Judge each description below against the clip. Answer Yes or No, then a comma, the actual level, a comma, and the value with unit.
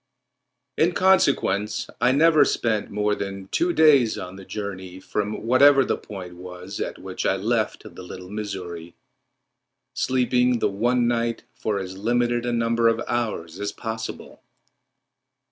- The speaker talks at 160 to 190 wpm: No, average, 145 wpm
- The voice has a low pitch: Yes, low, 110 Hz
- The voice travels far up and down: No, average, 4.0 semitones